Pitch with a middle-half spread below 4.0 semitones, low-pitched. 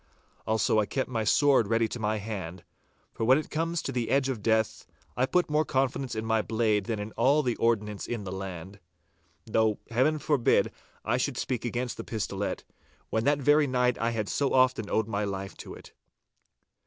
Yes: average, 3.6 semitones; low, 115 Hz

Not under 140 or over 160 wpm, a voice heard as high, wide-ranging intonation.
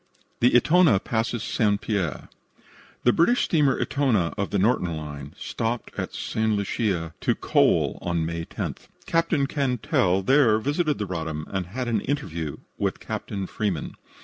No: average, 150 wpm; low, 105 Hz; wide, 6.5 semitones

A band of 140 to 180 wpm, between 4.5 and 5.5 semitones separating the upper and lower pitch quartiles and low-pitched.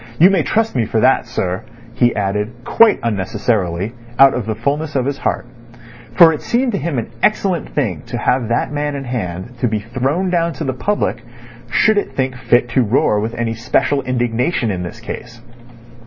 No: average, 195 wpm; average, 4.8 semitones; low, 125 Hz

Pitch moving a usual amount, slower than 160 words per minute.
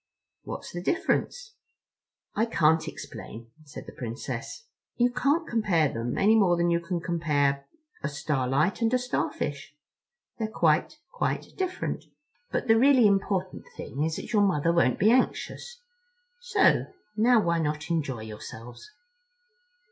No: wide, 7.5 semitones; average, 140 wpm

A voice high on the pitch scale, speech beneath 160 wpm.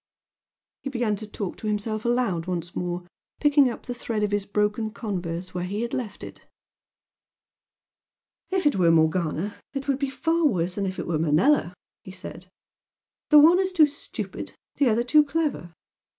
No: high, 210 Hz; average, 175 wpm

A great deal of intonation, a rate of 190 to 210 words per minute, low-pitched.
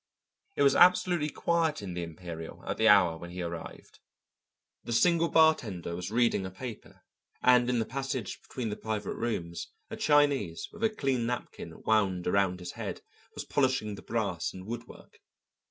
No: wide, 7.1 semitones; average, 170 wpm; low, 110 Hz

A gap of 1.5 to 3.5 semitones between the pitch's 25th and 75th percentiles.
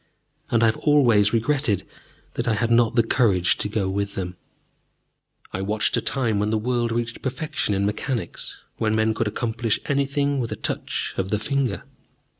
Yes: average, 3.2 semitones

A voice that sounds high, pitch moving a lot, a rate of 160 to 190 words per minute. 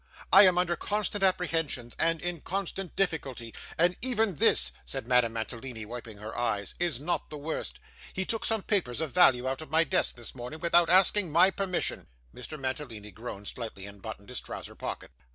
No: medium, 150 Hz; wide, 7.1 semitones; average, 185 wpm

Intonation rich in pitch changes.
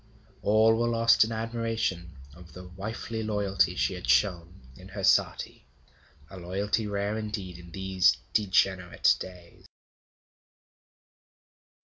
No: average, 3.6 semitones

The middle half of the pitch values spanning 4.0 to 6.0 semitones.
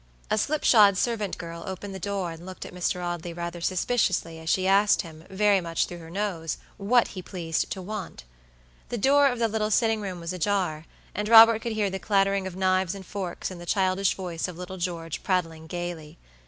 No: average, 3.0 semitones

